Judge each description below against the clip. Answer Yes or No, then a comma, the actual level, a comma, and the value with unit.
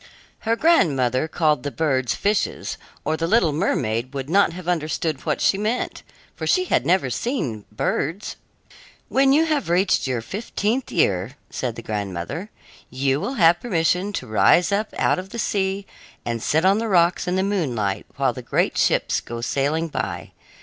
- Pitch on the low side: No, medium, 165 Hz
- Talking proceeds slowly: No, average, 170 wpm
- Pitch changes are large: Yes, wide, 7.6 semitones